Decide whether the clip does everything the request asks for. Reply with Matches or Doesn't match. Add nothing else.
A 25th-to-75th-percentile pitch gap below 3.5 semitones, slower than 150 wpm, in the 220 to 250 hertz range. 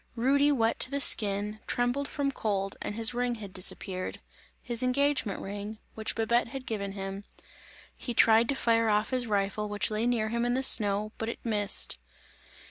Doesn't match